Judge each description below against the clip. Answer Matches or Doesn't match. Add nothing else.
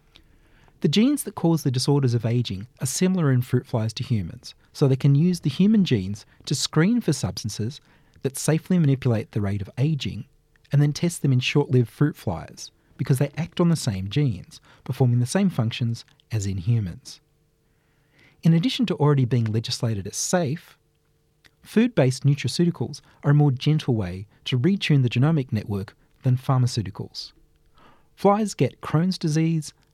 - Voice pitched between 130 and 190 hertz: Matches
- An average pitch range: Matches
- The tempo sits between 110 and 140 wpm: Doesn't match